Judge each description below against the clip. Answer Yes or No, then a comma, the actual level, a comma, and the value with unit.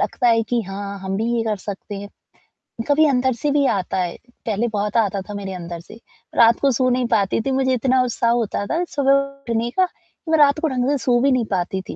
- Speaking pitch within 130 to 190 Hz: No, high, 235 Hz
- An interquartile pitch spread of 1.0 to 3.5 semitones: No, average, 4.9 semitones